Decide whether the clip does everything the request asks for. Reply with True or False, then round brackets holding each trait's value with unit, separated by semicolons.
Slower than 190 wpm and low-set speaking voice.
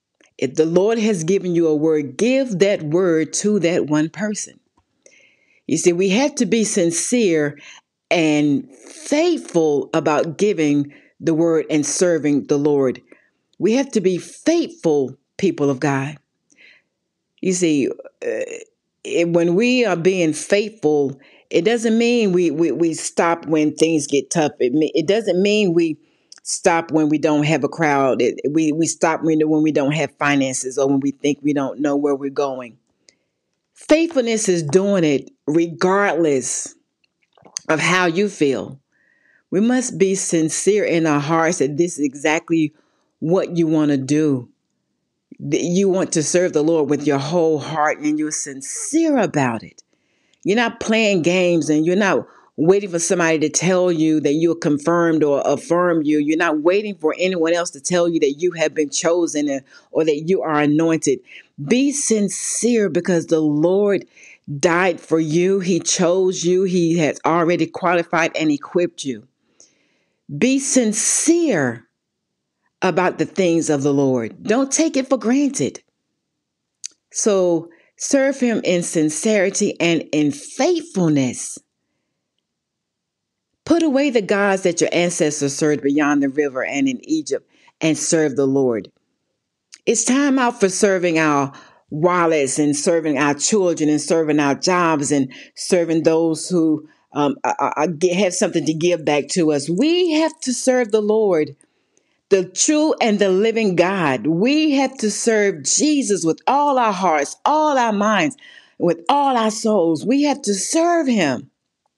False (155 wpm; 170 Hz)